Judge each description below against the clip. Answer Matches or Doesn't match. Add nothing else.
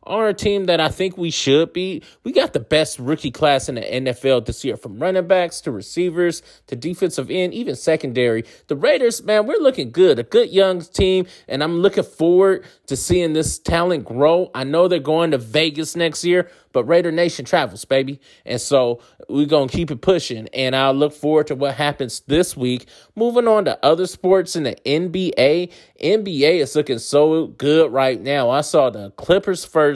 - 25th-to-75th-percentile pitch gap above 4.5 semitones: Matches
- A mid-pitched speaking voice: Matches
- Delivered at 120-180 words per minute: Doesn't match